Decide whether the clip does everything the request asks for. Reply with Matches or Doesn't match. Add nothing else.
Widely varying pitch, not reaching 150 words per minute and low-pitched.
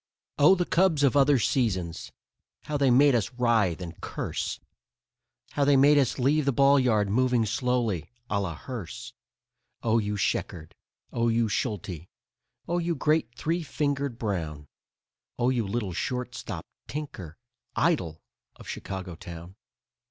Matches